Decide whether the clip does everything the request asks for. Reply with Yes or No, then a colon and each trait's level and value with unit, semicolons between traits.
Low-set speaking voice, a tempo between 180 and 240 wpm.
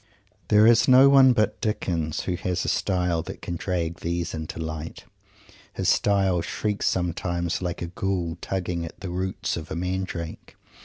No: very low, 90 Hz; average, 170 wpm